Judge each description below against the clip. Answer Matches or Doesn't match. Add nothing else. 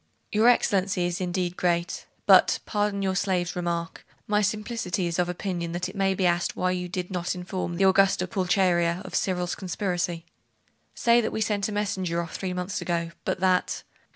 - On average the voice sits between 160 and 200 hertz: Matches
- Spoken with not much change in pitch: Matches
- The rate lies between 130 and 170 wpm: Doesn't match